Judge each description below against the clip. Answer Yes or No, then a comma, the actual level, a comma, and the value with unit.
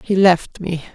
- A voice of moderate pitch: Yes, medium, 180 Hz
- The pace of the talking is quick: No, average, 190 wpm